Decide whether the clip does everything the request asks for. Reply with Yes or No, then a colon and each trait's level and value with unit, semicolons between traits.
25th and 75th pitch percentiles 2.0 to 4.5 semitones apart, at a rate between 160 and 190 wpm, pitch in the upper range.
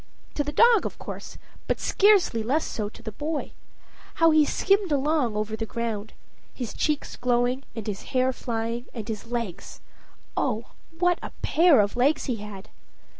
No: wide, 5.5 semitones; average, 170 wpm; high, 245 Hz